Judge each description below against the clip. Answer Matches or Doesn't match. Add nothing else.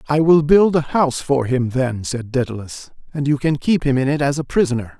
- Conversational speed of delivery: Doesn't match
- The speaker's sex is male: Matches